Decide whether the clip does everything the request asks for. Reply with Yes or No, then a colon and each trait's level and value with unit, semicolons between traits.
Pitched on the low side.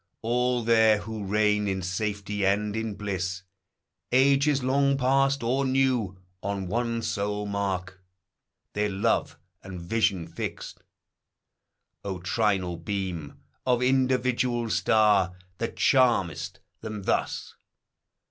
Yes: low, 105 Hz